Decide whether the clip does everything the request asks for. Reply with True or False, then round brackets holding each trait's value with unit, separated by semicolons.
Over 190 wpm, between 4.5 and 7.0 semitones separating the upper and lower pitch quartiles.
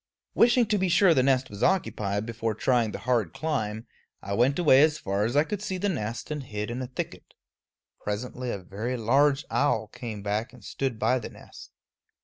True (200 wpm; 5.4 semitones)